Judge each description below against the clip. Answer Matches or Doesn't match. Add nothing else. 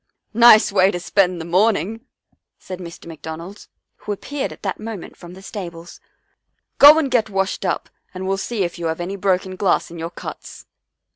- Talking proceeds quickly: Doesn't match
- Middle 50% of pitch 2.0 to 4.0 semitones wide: Matches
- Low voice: Doesn't match